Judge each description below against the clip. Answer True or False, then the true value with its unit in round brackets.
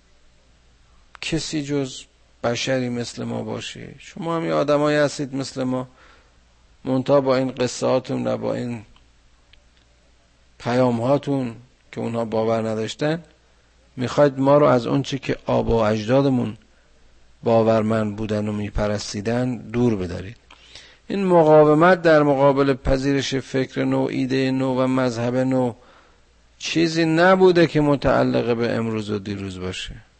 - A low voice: True (125 Hz)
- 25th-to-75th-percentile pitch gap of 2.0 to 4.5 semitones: False (5.4 semitones)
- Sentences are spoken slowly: False (115 wpm)